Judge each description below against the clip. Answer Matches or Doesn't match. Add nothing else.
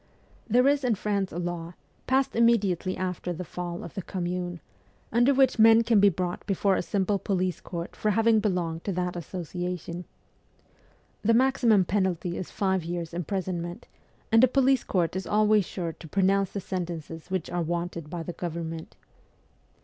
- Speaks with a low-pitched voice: Doesn't match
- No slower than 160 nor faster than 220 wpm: Matches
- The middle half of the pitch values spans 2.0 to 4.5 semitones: Matches